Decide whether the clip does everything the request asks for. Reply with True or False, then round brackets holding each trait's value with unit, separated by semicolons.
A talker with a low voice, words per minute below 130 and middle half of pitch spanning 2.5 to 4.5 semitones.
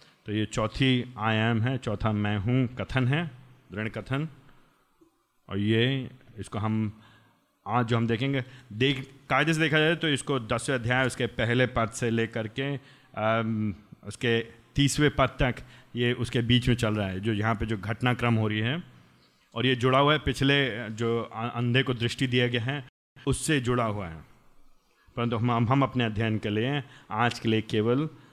False (120 Hz; 175 wpm; 3.0 semitones)